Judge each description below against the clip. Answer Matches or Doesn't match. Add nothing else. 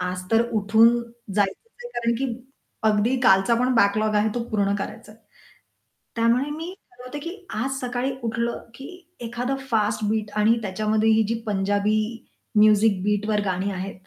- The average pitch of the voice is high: Matches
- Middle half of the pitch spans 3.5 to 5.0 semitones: Doesn't match